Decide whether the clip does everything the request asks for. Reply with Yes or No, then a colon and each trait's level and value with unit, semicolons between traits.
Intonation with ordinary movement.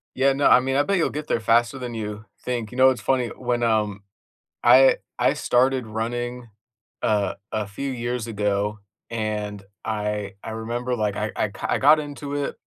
Yes: average, 3.4 semitones